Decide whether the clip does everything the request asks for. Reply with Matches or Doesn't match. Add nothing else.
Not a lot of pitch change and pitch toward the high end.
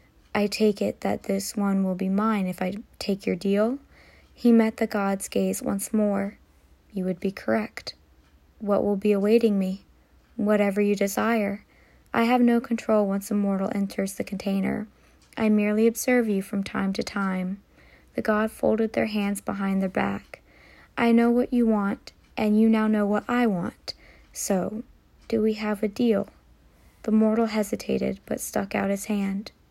Matches